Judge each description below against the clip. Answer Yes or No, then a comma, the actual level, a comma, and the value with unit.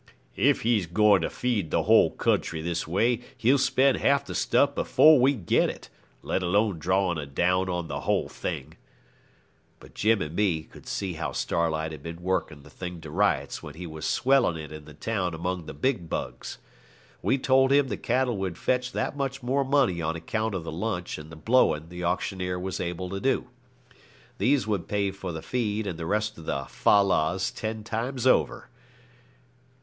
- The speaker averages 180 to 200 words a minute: Yes, average, 195 wpm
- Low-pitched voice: Yes, very low, 95 Hz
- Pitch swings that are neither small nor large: No, wide, 6.3 semitones